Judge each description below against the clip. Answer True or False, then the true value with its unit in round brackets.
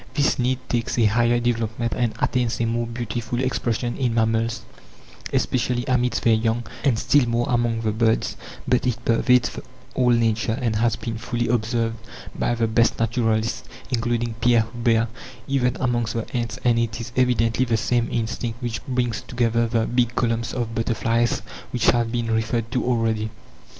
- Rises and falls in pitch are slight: True (1.1 semitones)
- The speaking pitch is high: False (115 Hz)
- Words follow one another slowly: False (165 wpm)